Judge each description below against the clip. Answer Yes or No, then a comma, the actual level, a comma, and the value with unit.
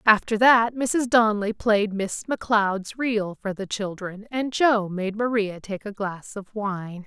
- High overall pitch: Yes, high, 210 Hz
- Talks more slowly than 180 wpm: Yes, average, 170 wpm